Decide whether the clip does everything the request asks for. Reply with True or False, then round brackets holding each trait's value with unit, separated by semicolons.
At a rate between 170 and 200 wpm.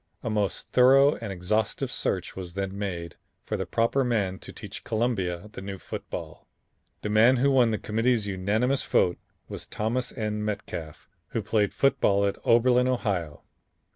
False (160 wpm)